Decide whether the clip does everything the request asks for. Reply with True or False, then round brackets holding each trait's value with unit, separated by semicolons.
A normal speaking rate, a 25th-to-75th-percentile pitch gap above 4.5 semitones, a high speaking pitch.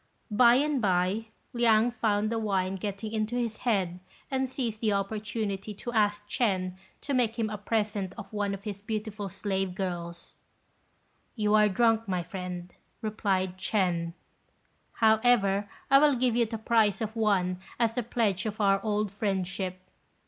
False (155 wpm; 2.7 semitones; 210 Hz)